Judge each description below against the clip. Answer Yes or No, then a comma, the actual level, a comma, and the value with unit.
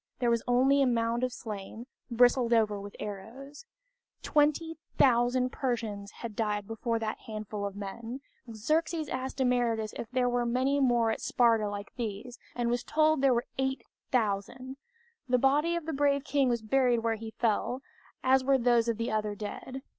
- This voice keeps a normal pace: Yes, average, 170 wpm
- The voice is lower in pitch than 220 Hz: No, high, 240 Hz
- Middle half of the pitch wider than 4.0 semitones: No, average, 3.1 semitones